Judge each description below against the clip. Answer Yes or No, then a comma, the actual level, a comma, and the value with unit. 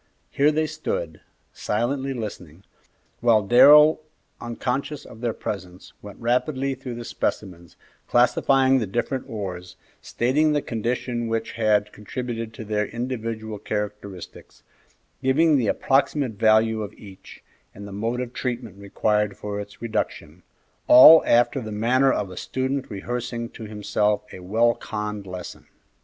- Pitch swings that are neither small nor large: Yes, average, 3.6 semitones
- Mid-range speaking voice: No, low, 115 Hz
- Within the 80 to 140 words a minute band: Yes, slow, 135 wpm